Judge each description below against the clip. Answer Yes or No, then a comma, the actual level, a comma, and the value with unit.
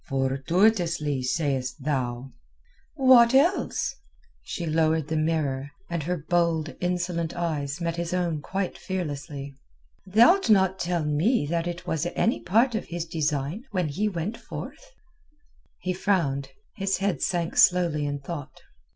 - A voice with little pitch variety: No, average, 4.1 semitones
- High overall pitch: No, medium, 170 Hz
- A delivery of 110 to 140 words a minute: Yes, slow, 135 wpm